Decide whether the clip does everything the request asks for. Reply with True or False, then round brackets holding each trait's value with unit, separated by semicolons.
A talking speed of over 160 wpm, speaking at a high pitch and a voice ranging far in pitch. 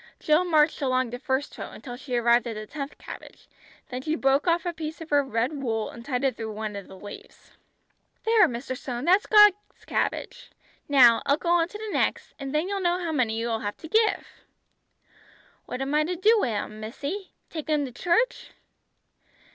True (205 wpm; 280 Hz; 6.1 semitones)